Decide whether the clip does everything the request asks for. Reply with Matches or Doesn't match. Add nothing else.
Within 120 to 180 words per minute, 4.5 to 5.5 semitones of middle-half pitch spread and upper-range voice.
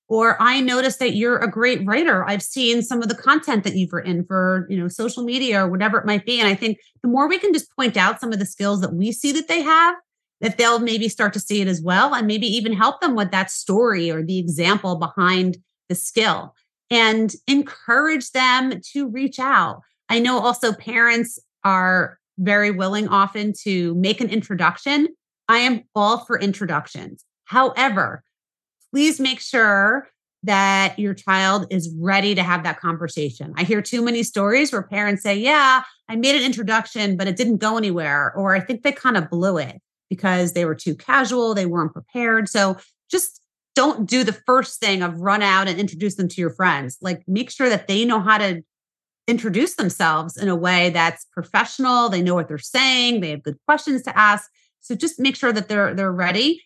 Doesn't match